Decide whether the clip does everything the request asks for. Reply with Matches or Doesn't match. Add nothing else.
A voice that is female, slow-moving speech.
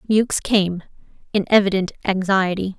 Matches